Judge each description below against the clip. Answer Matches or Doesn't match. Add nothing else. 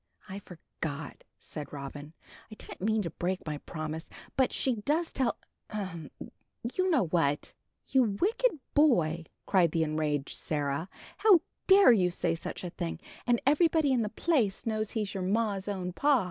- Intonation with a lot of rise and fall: Matches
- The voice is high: Matches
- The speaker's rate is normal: Matches